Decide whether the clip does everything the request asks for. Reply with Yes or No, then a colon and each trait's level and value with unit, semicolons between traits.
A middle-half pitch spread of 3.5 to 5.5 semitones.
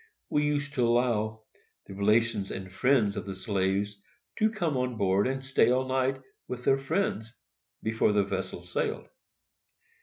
Yes: average, 4.8 semitones